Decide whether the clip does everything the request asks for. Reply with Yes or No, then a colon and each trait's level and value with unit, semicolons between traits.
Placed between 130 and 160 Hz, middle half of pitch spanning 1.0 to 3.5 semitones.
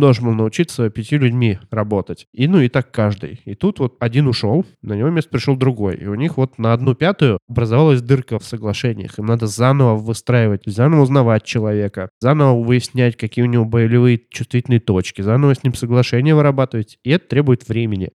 No: low, 120 Hz; average, 3.2 semitones